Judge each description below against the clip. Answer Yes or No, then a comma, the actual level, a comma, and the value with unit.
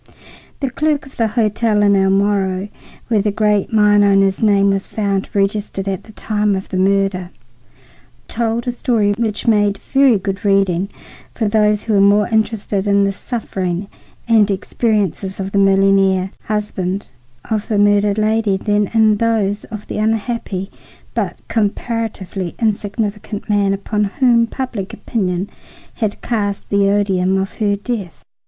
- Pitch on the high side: Yes, high, 205 Hz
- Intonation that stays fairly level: Yes, narrow, 1.9 semitones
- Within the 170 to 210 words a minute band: No, average, 150 wpm